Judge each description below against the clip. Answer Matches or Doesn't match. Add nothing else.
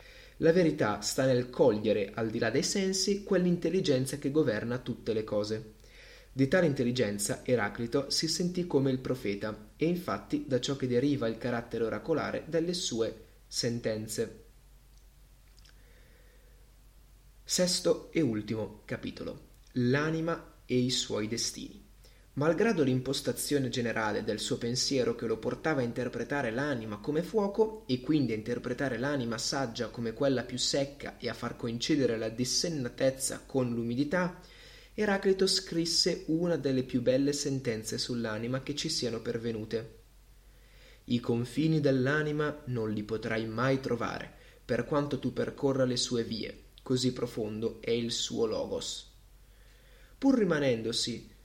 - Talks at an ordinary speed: Matches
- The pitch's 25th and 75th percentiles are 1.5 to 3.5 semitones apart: Doesn't match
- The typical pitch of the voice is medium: Doesn't match